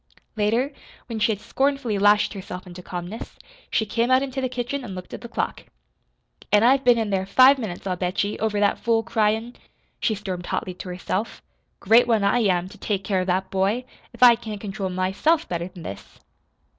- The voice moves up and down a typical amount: Yes, average, 4.0 semitones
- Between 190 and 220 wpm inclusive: Yes, fast, 205 wpm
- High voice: Yes, high, 210 Hz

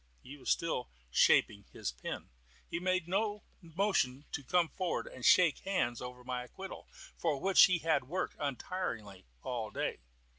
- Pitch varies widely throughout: Yes, wide, 6.7 semitones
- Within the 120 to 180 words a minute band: Yes, average, 155 wpm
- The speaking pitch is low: No, medium, 150 Hz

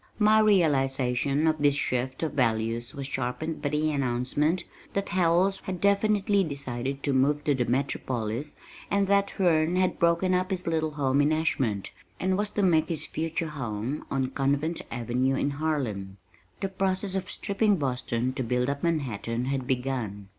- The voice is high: No, medium, 145 Hz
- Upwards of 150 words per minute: Yes, average, 165 wpm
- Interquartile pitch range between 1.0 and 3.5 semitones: No, wide, 5.4 semitones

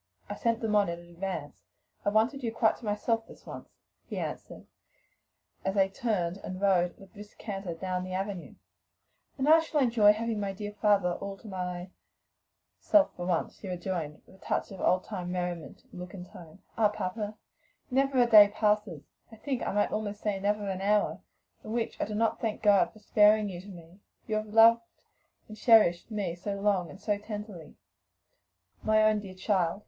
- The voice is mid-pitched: No, high, 205 Hz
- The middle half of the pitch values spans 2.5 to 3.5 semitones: Yes, average, 2.8 semitones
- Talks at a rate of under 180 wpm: No, average, 195 wpm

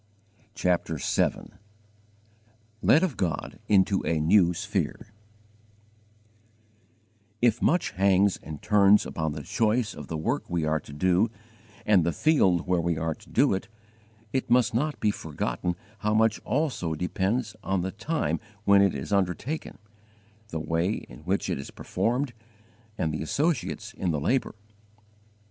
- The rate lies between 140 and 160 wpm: Yes, average, 145 wpm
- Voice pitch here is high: No, very low, 95 Hz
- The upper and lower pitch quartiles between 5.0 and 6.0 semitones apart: Yes, wide, 5.5 semitones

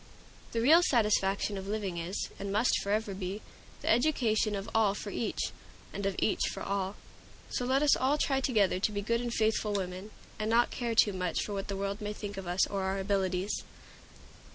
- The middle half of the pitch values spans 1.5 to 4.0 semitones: Yes, narrow, 2.6 semitones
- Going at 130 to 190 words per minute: No, fast, 205 wpm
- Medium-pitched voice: No, high, 205 Hz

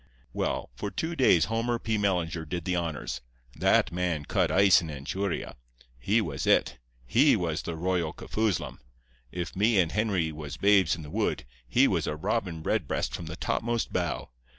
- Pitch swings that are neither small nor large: Yes, average, 4.7 semitones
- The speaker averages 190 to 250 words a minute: No, average, 175 wpm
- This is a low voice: Yes, very low, 90 Hz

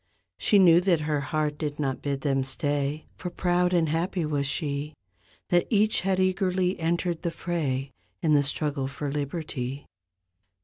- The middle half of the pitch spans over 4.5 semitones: No, average, 3.6 semitones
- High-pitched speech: No, medium, 155 Hz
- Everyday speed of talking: Yes, average, 160 wpm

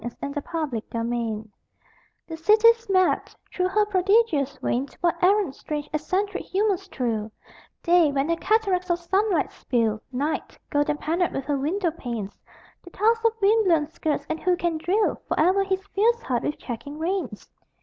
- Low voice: No, very high, 335 Hz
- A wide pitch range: Yes, wide, 5.7 semitones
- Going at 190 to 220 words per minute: No, average, 160 wpm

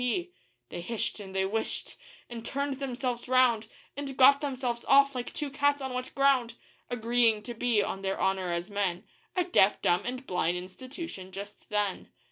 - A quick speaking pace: No, average, 175 wpm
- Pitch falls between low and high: No, high, 240 Hz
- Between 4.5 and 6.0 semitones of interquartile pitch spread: Yes, average, 5.1 semitones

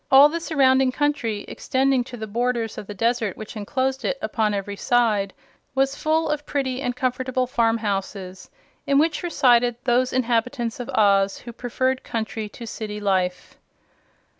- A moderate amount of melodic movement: Yes, average, 3.5 semitones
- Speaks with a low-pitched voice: No, high, 245 Hz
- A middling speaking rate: Yes, average, 155 wpm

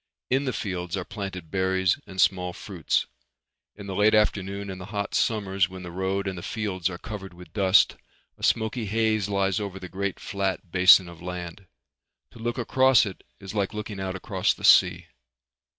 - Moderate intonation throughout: No, narrow, 2.2 semitones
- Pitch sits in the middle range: No, very low, 95 Hz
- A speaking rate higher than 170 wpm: Yes, average, 185 wpm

